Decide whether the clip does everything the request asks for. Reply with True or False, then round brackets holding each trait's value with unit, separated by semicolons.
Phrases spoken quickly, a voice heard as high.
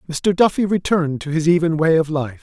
False (225 wpm; 165 Hz)